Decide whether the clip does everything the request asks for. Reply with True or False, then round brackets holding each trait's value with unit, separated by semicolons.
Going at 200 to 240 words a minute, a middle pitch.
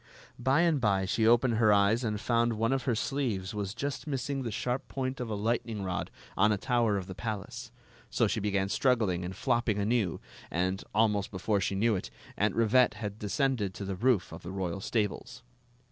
False (205 wpm; 110 Hz)